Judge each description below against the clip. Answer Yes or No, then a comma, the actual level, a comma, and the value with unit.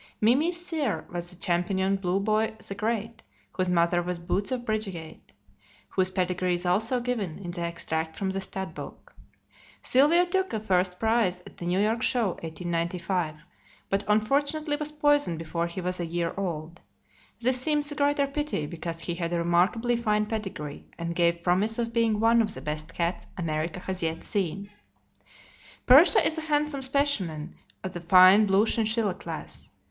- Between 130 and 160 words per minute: No, average, 170 wpm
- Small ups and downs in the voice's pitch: No, average, 5.3 semitones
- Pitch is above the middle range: Yes, high, 195 Hz